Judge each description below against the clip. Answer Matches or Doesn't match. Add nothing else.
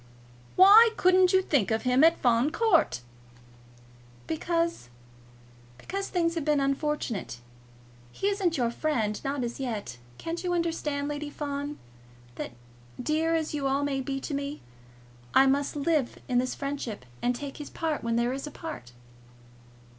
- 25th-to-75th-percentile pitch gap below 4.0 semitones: Doesn't match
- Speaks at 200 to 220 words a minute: Doesn't match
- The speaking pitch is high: Matches